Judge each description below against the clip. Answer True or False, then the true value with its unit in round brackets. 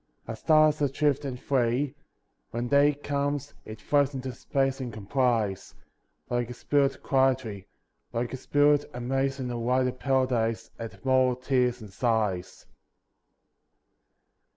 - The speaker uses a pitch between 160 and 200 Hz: False (130 Hz)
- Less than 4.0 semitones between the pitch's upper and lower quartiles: True (2.9 semitones)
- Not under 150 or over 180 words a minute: False (135 wpm)